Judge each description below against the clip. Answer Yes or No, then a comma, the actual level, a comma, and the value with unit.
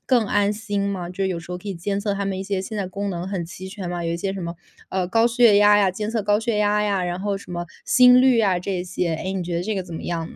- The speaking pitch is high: Yes, high, 195 Hz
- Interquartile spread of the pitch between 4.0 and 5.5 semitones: No, narrow, 2.6 semitones